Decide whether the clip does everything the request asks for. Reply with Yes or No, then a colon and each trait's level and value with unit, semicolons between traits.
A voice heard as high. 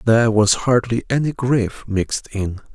No: low, 115 Hz